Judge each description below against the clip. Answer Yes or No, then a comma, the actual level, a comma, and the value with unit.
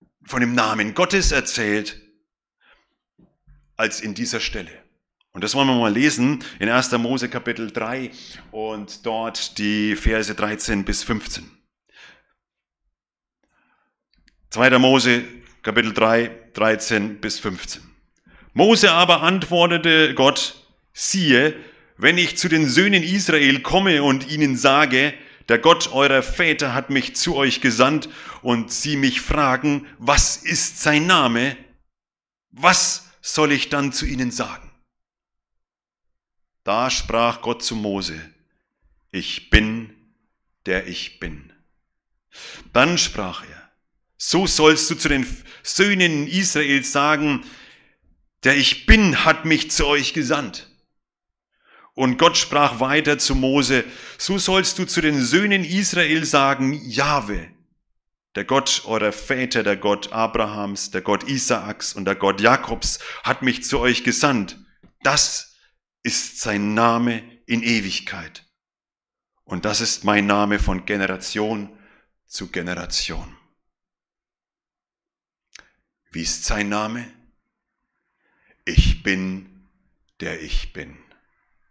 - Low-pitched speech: Yes, low, 125 Hz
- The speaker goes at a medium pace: No, slow, 115 wpm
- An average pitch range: No, wide, 6.0 semitones